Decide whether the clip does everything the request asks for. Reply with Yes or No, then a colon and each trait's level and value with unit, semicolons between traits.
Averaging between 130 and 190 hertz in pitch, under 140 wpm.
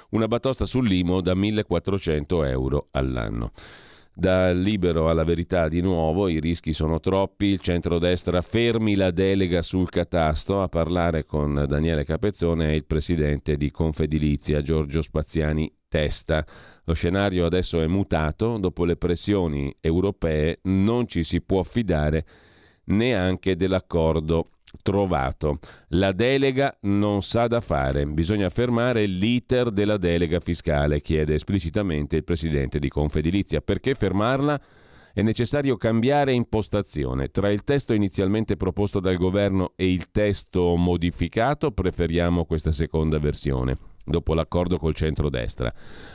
No: very low, 90 Hz; average, 125 wpm